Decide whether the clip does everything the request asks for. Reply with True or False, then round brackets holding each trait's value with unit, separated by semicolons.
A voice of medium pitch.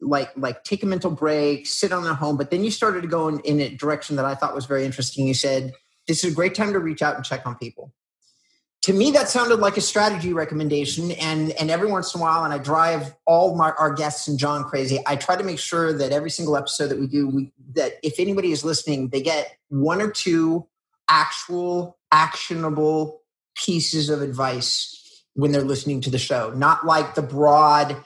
True (155 Hz)